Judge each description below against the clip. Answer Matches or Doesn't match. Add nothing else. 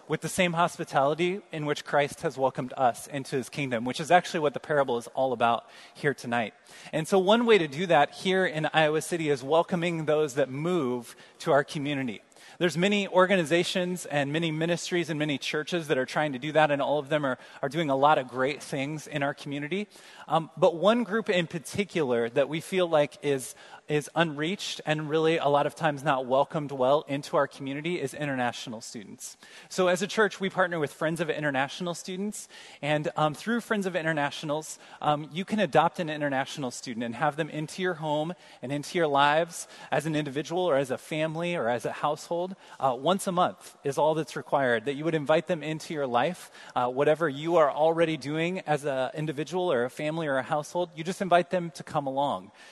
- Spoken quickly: Matches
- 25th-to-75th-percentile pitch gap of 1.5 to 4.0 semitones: Matches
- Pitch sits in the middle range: Matches